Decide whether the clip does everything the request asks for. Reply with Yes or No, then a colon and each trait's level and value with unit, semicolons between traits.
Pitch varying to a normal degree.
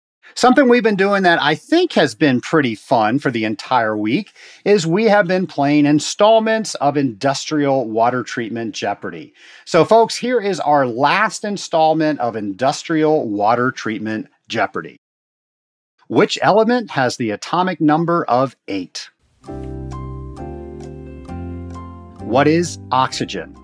No: wide, 8.8 semitones